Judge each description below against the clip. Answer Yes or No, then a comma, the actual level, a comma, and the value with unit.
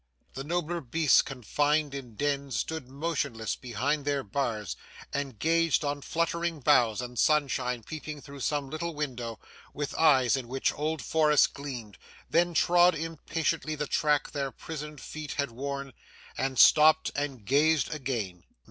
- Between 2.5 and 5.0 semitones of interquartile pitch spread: Yes, average, 3.2 semitones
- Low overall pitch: No, medium, 145 Hz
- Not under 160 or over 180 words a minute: No, average, 145 wpm